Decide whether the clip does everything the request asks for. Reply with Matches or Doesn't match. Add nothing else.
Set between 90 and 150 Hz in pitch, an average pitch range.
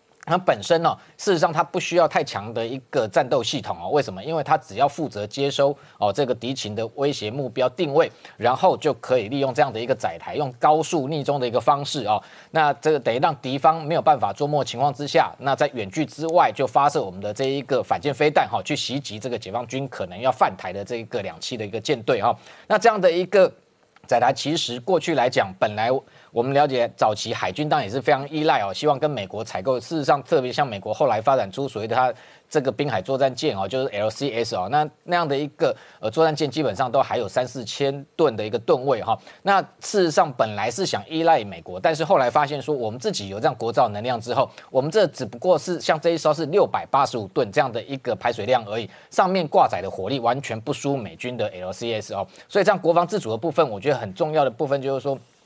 Matches